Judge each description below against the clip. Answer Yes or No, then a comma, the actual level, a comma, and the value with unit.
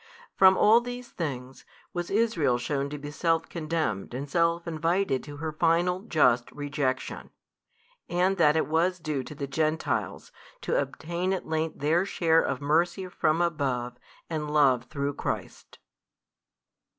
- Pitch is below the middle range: No, medium, 155 Hz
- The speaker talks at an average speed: Yes, average, 150 wpm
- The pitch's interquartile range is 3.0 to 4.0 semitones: Yes, average, 3.5 semitones